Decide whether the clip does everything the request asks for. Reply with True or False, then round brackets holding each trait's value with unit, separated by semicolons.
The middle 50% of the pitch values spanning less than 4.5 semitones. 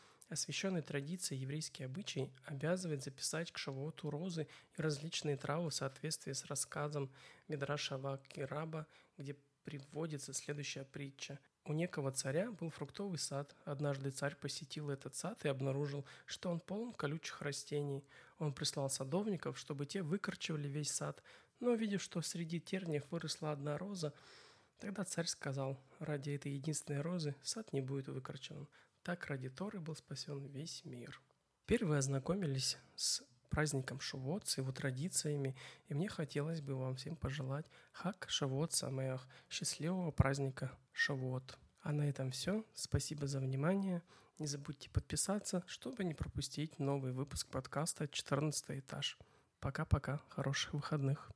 True (3.0 semitones)